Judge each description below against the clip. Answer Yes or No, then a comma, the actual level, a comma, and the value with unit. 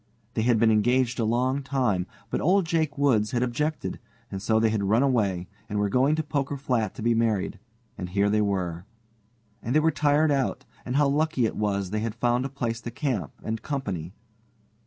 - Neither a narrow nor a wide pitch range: Yes, average, 4.8 semitones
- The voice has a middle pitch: No, low, 120 Hz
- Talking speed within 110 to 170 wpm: No, fast, 205 wpm